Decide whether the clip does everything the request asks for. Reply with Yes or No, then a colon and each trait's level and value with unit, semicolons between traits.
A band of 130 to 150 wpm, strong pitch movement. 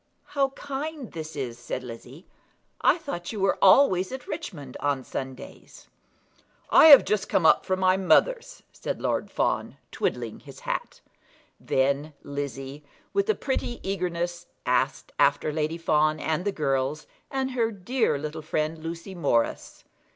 Yes: average, 145 wpm; wide, 8.3 semitones